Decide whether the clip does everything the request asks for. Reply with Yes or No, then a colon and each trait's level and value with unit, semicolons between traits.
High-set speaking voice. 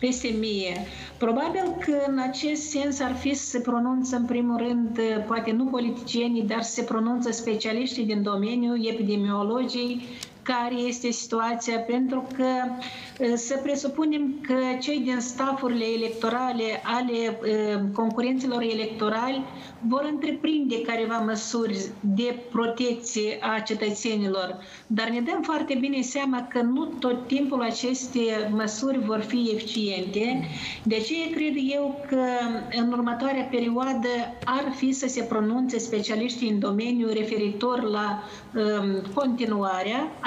Yes: high, 240 Hz